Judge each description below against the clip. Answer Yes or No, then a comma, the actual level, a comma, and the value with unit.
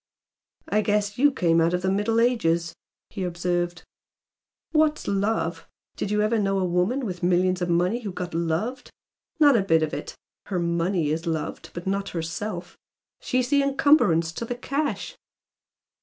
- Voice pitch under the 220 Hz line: Yes, high, 190 Hz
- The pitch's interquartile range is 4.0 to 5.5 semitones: Yes, average, 4.9 semitones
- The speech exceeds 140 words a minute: Yes, average, 165 wpm